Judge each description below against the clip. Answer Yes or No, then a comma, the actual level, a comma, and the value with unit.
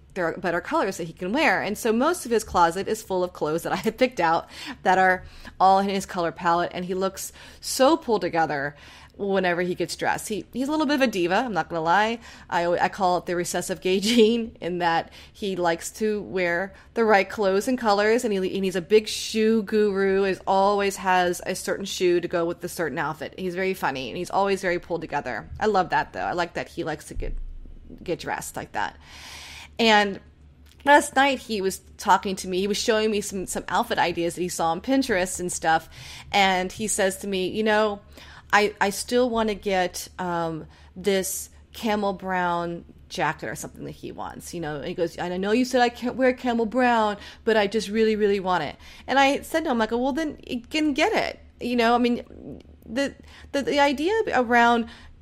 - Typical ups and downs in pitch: Yes, average, 4.1 semitones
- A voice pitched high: Yes, high, 195 Hz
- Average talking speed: No, fast, 220 wpm